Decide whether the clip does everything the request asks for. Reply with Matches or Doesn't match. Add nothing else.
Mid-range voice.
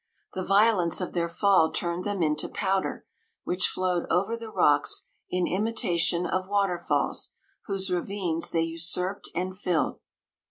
Matches